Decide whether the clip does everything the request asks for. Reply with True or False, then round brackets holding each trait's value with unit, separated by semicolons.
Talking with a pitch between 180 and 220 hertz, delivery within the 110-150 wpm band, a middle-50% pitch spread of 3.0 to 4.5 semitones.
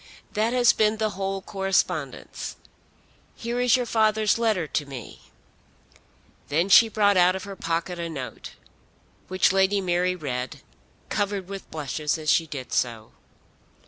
False (190 Hz; 145 wpm; 5.1 semitones)